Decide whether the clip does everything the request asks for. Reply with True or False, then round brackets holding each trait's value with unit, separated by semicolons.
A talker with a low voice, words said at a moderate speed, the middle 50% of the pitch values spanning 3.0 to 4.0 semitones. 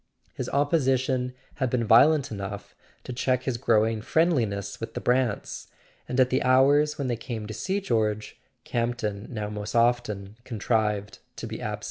True (120 Hz; 160 wpm; 3.4 semitones)